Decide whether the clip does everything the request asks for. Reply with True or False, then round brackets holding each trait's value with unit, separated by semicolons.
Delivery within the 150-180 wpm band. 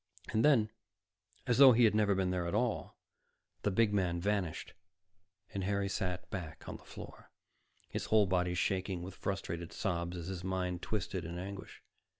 True (170 wpm)